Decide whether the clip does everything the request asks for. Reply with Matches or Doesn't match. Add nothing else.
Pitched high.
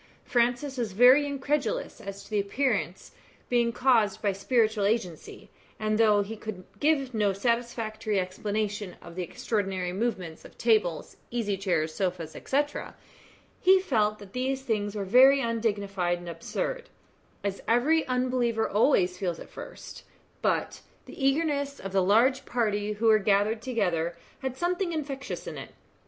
Matches